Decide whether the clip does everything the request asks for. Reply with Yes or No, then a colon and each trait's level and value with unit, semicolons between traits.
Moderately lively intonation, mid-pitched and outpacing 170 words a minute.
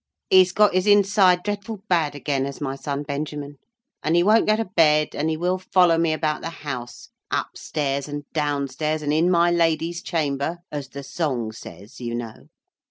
Yes: average, 3.9 semitones; medium, 155 Hz; average, 185 wpm